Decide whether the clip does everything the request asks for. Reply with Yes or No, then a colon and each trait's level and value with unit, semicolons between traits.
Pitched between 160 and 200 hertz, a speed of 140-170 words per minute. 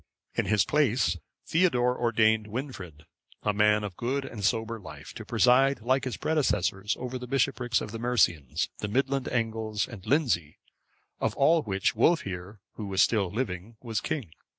No: low, 115 Hz; average, 160 wpm